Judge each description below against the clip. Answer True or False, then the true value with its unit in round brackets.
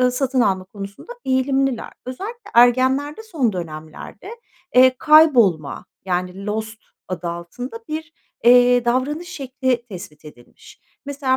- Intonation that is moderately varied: False (5.8 semitones)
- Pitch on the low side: False (250 Hz)